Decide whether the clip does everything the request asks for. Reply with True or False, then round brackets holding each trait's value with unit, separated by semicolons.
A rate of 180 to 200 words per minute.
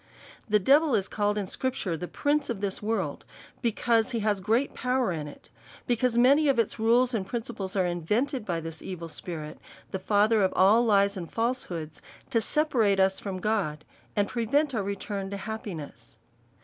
True (190 wpm)